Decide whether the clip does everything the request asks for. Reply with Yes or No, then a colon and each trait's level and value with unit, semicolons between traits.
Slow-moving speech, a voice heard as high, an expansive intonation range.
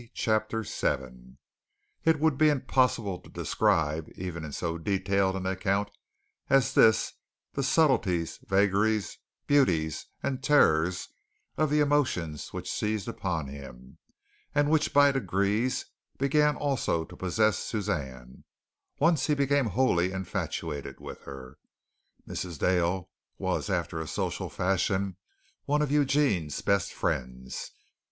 No: slow, 120 wpm; low, 100 Hz; wide, 8.4 semitones